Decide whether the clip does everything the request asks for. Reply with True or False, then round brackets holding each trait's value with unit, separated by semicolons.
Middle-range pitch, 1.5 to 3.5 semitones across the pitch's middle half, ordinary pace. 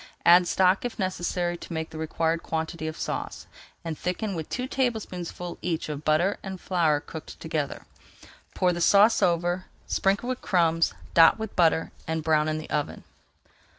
True (170 Hz; 2.7 semitones; 165 wpm)